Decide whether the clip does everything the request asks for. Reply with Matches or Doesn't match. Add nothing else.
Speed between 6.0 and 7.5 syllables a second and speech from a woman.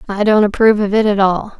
Matches